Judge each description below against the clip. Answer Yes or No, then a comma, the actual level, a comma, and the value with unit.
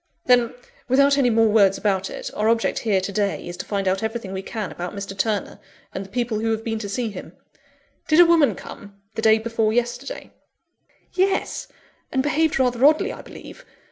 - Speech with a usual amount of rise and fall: Yes, average, 4.0 semitones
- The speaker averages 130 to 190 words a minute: No, average, 200 wpm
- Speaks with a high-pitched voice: Yes, high, 225 Hz